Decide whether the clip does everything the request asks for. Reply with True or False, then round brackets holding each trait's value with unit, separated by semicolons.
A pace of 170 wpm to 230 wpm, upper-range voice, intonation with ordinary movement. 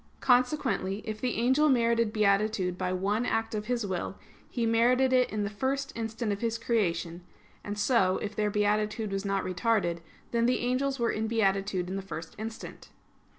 True (180 wpm; 215 Hz; 3.1 semitones)